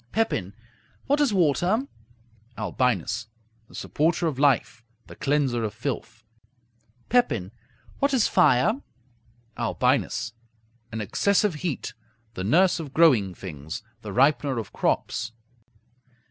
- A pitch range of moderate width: No, wide, 8.5 semitones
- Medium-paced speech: No, slow, 110 wpm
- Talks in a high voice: No, medium, 140 Hz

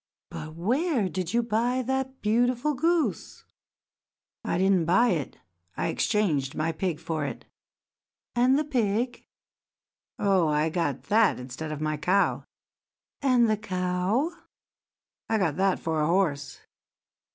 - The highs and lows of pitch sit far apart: Yes, wide, 7.2 semitones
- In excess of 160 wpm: No, slow, 135 wpm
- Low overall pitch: No, high, 195 Hz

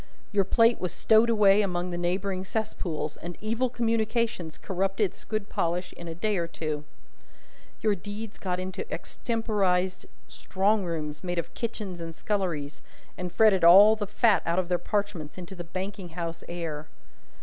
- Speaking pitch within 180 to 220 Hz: Yes, high, 190 Hz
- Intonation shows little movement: No, average, 3.6 semitones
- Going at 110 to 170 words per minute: Yes, average, 160 wpm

